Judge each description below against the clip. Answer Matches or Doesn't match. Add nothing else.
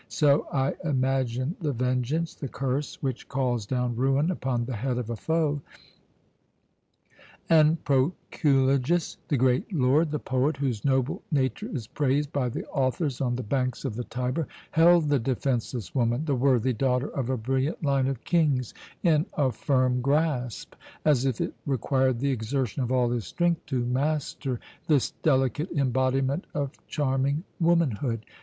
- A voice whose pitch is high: Doesn't match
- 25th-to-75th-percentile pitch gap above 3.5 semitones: Doesn't match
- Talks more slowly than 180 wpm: Matches